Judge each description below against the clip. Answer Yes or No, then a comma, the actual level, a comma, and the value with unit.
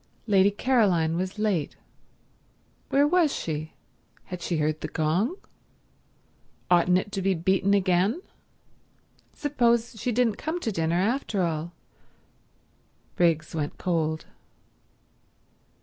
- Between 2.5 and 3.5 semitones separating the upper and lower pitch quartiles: No, wide, 5.6 semitones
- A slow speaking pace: Yes, slow, 110 wpm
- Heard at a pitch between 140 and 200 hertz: Yes, high, 190 Hz